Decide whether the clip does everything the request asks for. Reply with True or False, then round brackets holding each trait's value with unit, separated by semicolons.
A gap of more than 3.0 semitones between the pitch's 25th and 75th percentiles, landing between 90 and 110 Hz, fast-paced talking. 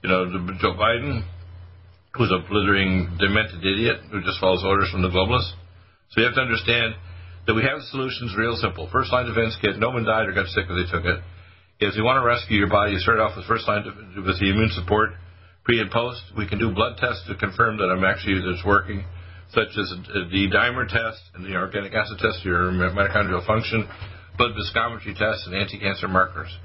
True (3.4 semitones; 100 Hz; 215 wpm)